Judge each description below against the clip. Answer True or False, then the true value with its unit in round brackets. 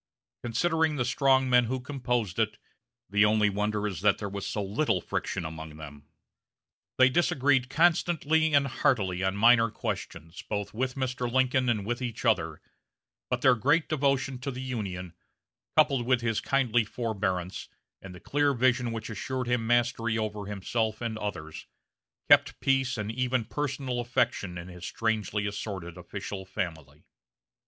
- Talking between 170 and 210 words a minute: False (155 wpm)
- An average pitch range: True (4.4 semitones)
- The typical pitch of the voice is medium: False (115 Hz)